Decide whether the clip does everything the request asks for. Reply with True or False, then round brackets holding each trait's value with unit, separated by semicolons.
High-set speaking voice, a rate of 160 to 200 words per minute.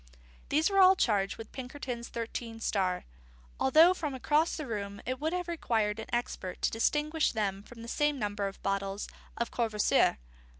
True (235 Hz; 170 wpm)